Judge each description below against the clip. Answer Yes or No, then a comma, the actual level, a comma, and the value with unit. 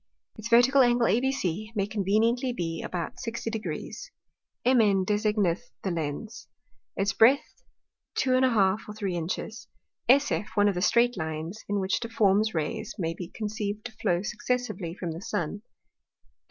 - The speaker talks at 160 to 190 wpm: No, average, 140 wpm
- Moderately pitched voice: No, high, 210 Hz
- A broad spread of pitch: No, average, 3.9 semitones